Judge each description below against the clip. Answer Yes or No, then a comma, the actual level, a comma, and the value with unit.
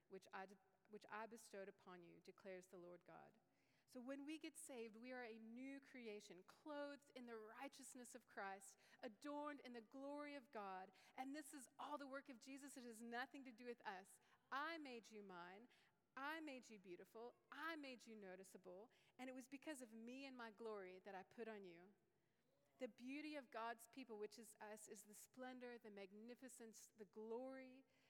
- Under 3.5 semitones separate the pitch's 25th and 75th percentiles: No, average, 4.2 semitones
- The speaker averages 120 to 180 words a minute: No, average, 190 wpm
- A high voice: Yes, high, 235 Hz